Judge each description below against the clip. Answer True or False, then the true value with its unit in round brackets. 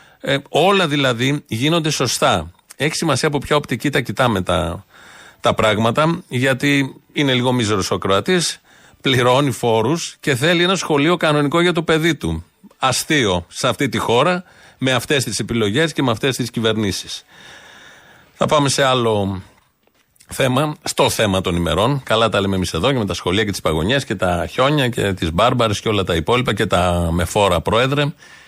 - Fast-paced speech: True (175 wpm)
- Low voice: True (130 Hz)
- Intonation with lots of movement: True (6.6 semitones)